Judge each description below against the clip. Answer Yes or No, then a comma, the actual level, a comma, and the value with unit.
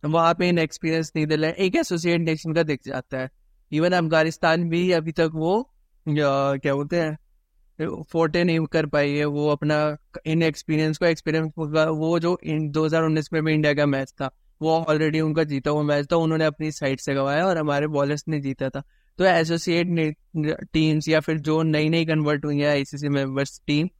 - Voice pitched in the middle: Yes, medium, 155 Hz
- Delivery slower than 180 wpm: No, average, 185 wpm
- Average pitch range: No, narrow, 1.8 semitones